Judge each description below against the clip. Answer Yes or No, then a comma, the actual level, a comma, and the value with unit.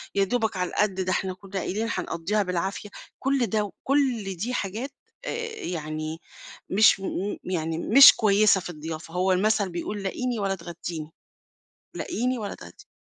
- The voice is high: Yes, high, 195 Hz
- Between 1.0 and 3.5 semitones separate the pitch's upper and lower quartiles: No, average, 3.9 semitones